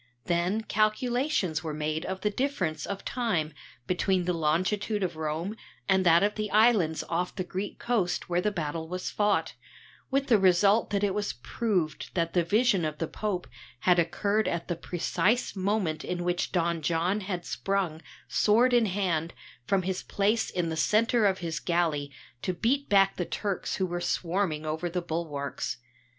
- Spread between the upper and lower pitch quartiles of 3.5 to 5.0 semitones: Yes, average, 3.8 semitones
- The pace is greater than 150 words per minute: Yes, average, 175 wpm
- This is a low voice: No, medium, 185 Hz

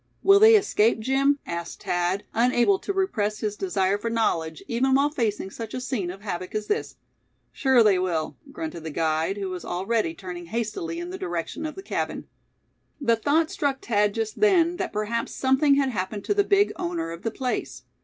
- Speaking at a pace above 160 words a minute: Yes, average, 195 wpm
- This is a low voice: No, high, 225 Hz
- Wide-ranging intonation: Yes, wide, 7.2 semitones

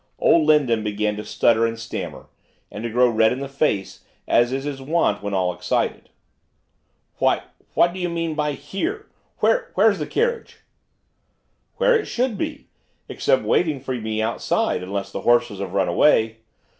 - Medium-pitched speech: No, low, 125 Hz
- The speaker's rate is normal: Yes, average, 170 wpm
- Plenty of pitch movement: Yes, wide, 7.5 semitones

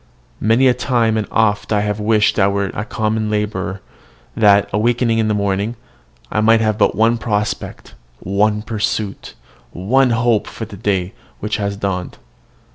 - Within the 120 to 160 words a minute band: Yes, average, 155 wpm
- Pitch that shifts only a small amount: Yes, narrow, 1.9 semitones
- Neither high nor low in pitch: No, low, 105 Hz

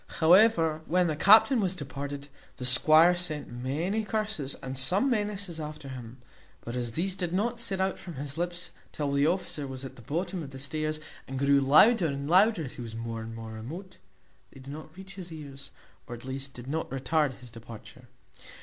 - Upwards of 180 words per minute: Yes, average, 200 wpm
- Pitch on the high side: No, medium, 150 Hz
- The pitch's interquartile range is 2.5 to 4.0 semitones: No, average, 5.3 semitones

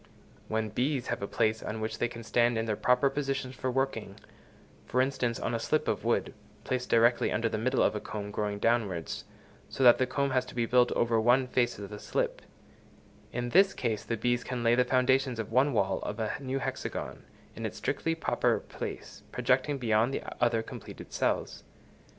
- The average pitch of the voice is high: No, low, 120 Hz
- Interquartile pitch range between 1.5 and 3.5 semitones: Yes, narrow, 2.6 semitones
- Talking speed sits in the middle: Yes, average, 195 wpm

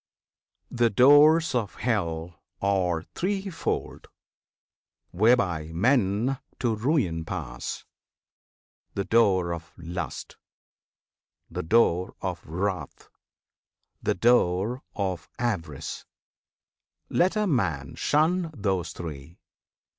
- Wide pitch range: Yes, wide, 6.4 semitones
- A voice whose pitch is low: Yes, low, 100 Hz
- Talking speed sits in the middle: No, slow, 85 wpm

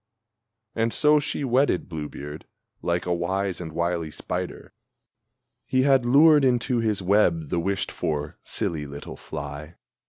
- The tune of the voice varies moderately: No, wide, 7.4 semitones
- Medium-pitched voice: No, very low, 95 Hz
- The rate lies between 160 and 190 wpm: No, average, 145 wpm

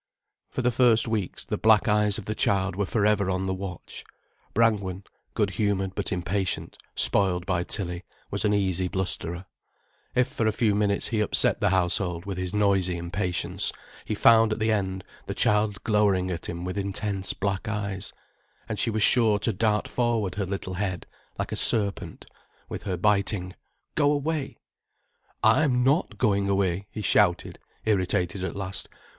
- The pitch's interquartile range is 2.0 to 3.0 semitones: Yes, narrow, 2.5 semitones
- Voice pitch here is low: Yes, low, 100 Hz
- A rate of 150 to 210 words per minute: Yes, average, 170 wpm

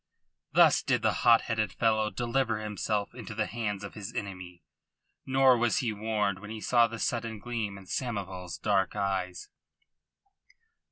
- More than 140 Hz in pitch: No, low, 105 Hz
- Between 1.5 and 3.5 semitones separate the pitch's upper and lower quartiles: Yes, average, 2.7 semitones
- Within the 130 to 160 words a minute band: Yes, average, 155 wpm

